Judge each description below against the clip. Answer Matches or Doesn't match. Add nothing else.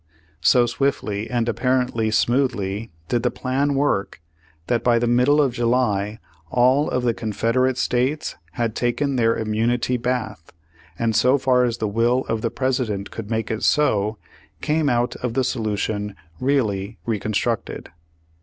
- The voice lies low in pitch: Matches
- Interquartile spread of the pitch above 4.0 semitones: Doesn't match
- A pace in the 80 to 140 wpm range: Doesn't match